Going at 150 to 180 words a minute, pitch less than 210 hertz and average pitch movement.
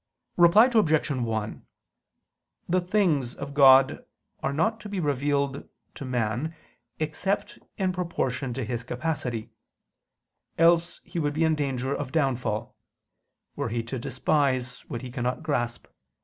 No: slow, 135 wpm; medium, 140 Hz; average, 4.6 semitones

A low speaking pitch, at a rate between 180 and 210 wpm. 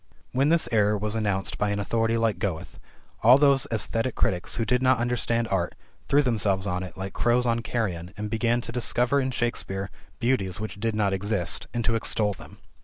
Yes: low, 110 Hz; average, 195 wpm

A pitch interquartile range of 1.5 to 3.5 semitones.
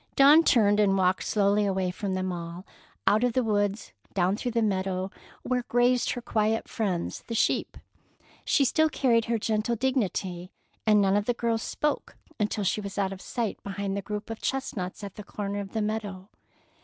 Yes: average, 3.1 semitones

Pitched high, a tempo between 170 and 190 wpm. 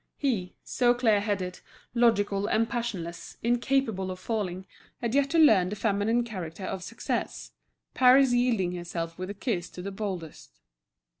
No: high, 205 Hz; average, 150 wpm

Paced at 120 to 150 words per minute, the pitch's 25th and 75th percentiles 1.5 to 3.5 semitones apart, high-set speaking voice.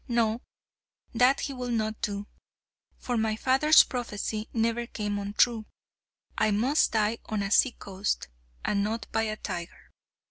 Yes: average, 145 wpm; narrow, 2.4 semitones; high, 220 Hz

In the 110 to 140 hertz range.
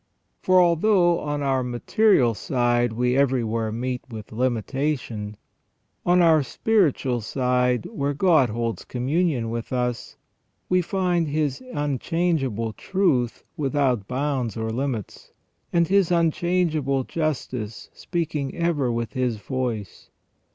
Yes: low, 135 Hz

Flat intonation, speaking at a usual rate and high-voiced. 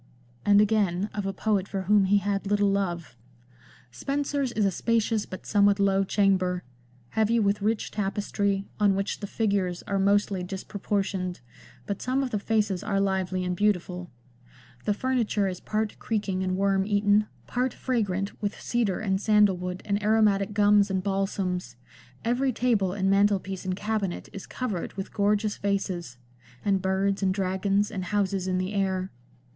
Yes: narrow, 1.8 semitones; average, 165 wpm; high, 200 Hz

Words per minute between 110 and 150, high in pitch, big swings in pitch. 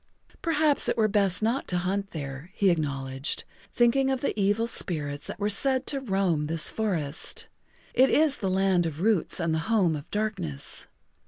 No: average, 175 wpm; high, 195 Hz; wide, 6.0 semitones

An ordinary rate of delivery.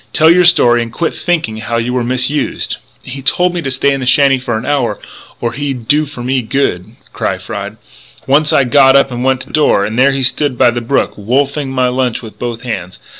No: fast, 230 wpm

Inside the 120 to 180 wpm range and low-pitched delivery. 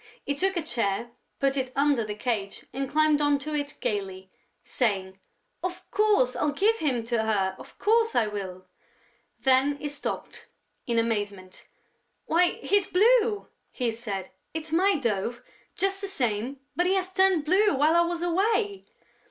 No: average, 160 wpm; very high, 285 Hz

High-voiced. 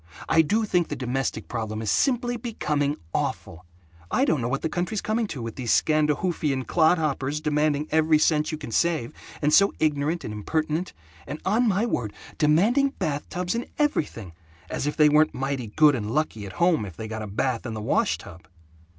No: medium, 150 Hz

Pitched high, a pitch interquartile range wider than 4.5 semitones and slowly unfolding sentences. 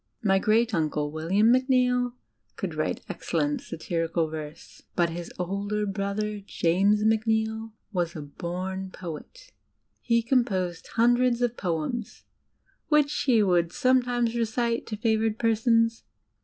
Yes: high, 215 Hz; average, 5.0 semitones; slow, 120 wpm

